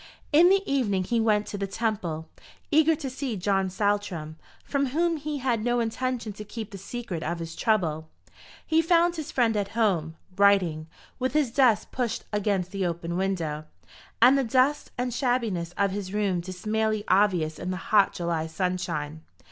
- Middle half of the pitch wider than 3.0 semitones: Yes, wide, 5.6 semitones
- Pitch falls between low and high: No, high, 205 Hz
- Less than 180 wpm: Yes, average, 170 wpm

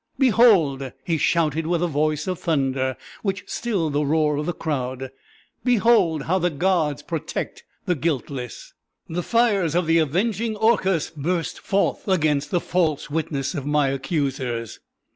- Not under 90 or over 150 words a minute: Yes, average, 145 wpm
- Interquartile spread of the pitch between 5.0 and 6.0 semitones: No, average, 4.4 semitones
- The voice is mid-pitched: Yes, medium, 160 Hz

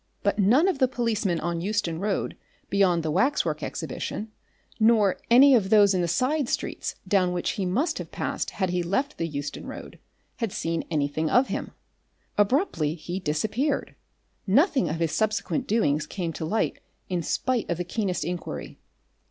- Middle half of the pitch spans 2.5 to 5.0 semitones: No, wide, 5.5 semitones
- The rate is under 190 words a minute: Yes, average, 170 wpm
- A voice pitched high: Yes, high, 195 Hz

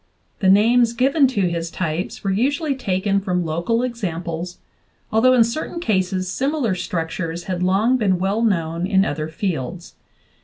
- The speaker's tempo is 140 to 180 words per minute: Yes, average, 150 wpm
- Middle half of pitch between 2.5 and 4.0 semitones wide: No, average, 5.1 semitones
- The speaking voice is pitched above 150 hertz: Yes, high, 190 Hz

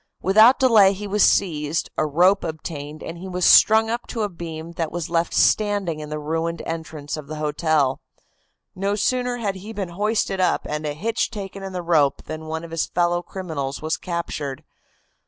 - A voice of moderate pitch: Yes, medium, 170 Hz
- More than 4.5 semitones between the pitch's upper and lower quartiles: No, average, 4.2 semitones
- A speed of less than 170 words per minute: No, average, 190 wpm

